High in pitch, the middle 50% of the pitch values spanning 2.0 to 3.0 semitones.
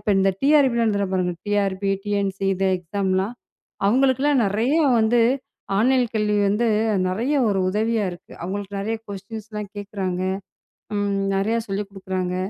Yes: high, 205 Hz; narrow, 2.5 semitones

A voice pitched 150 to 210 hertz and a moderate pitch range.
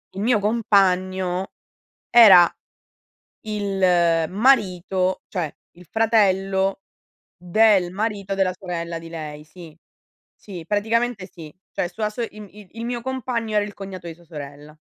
Yes: high, 190 Hz; average, 3.5 semitones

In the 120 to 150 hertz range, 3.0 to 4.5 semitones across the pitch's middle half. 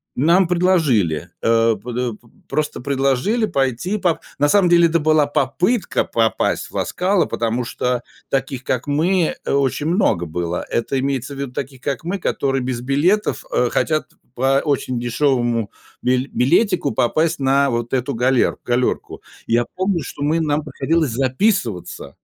No: low, 135 Hz; average, 5.1 semitones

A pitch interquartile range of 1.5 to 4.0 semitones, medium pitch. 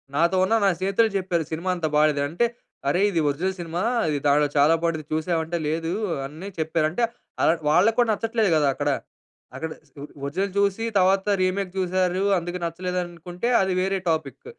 Yes: average, 3.1 semitones; medium, 175 Hz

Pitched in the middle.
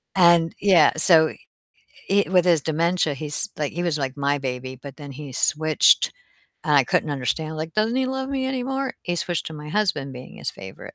Yes: medium, 160 Hz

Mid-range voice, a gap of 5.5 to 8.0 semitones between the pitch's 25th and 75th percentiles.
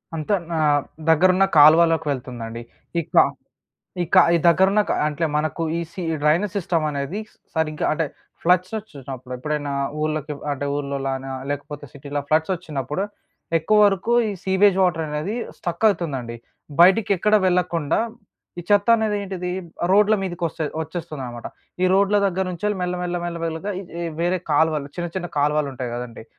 No: medium, 165 Hz; average, 4.2 semitones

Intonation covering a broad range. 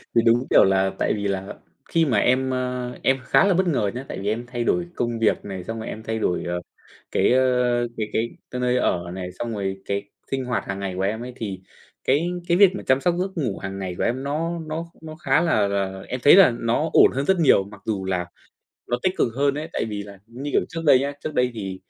Yes: wide, 6.0 semitones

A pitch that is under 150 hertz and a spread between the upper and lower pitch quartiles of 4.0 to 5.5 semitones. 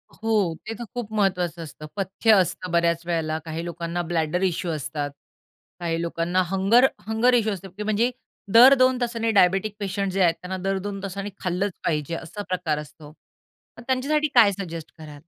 No: medium, 185 Hz; average, 4.4 semitones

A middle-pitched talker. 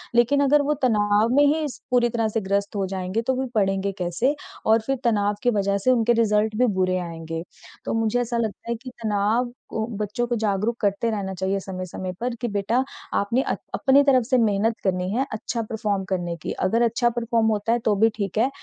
No: high, 220 Hz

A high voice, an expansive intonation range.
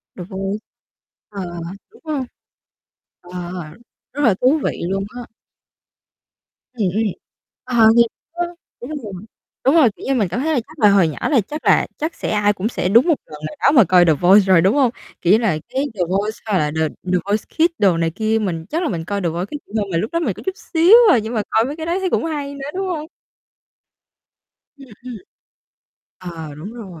Yes: high, 220 Hz; wide, 7.5 semitones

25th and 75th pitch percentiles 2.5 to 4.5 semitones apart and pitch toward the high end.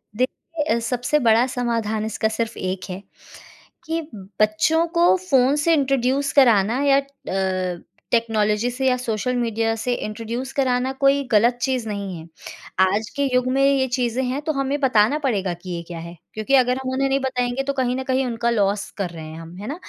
Yes: average, 4.0 semitones; high, 245 Hz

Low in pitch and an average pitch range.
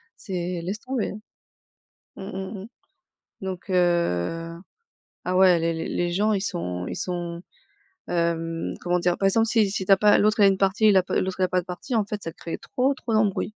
No: medium, 185 Hz; average, 3.1 semitones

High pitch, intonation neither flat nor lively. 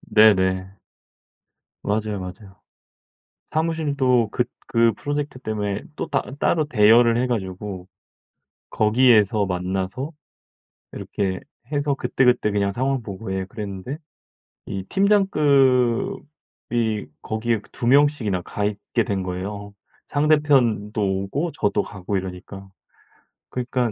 No: low, 110 Hz; average, 4.9 semitones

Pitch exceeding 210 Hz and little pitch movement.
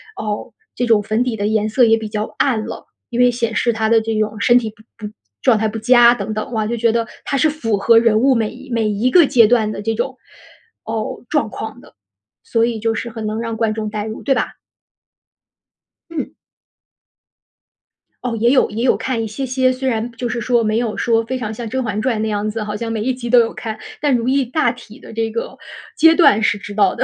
Yes: high, 225 Hz; narrow, 2.2 semitones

